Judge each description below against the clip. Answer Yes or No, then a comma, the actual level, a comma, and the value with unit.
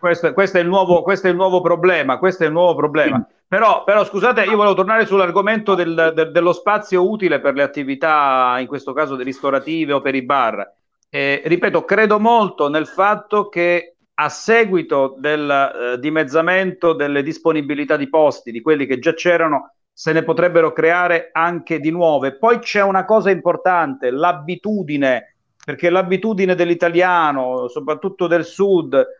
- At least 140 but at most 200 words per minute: Yes, average, 160 wpm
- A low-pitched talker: No, medium, 170 Hz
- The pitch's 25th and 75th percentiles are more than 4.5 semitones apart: No, average, 4.1 semitones